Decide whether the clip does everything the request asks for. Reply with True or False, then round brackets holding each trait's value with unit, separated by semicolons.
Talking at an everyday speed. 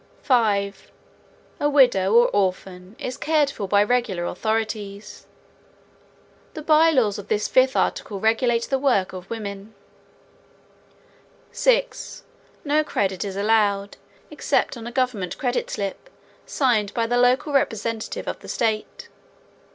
False (130 wpm)